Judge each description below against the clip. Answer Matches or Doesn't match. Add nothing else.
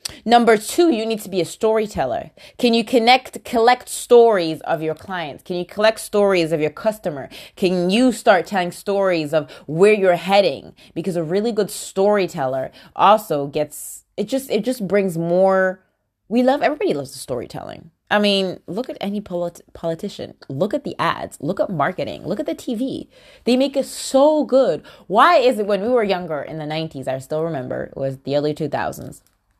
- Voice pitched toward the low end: Doesn't match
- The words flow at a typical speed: Matches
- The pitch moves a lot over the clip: Matches